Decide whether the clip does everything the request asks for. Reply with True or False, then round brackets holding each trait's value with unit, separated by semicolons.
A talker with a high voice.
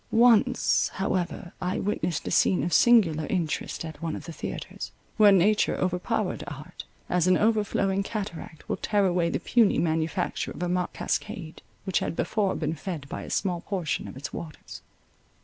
False (180 Hz)